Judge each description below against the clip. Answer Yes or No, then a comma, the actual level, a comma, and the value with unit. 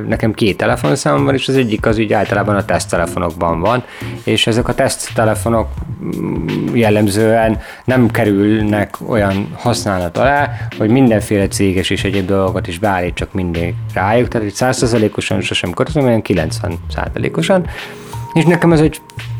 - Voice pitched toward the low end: Yes, low, 110 Hz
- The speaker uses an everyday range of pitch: Yes, average, 3.4 semitones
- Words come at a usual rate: Yes, average, 140 wpm